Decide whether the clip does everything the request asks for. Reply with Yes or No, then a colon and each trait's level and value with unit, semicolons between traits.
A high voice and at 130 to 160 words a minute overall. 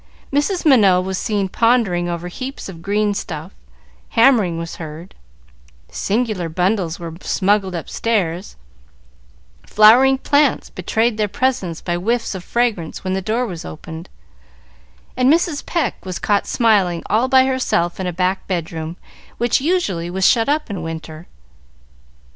Yes: high, 195 Hz; average, 140 wpm